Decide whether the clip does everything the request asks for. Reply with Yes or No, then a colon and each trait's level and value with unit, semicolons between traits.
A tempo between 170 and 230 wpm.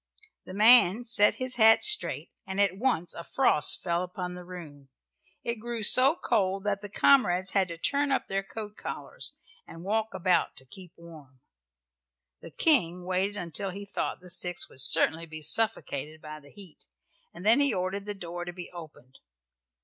Yes: average, 180 wpm